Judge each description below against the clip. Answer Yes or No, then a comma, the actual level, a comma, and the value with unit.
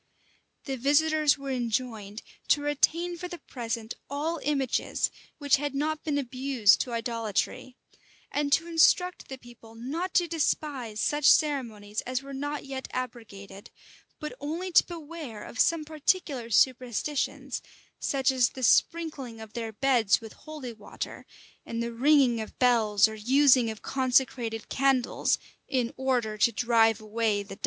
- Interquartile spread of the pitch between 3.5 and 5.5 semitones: Yes, average, 4.2 semitones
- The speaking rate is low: No, average, 145 wpm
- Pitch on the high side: Yes, very high, 255 Hz